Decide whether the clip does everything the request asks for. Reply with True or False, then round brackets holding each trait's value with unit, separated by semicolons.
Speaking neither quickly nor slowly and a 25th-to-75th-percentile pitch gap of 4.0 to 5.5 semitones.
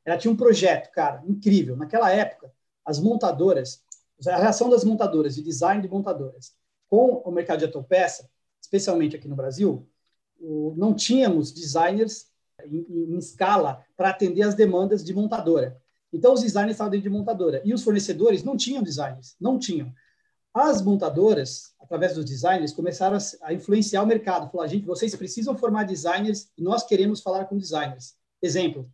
True (165 wpm; 5.0 semitones)